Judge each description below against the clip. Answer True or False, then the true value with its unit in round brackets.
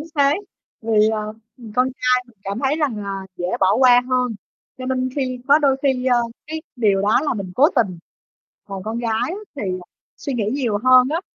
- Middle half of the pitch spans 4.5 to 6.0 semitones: False (3.9 semitones)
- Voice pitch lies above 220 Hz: True (245 Hz)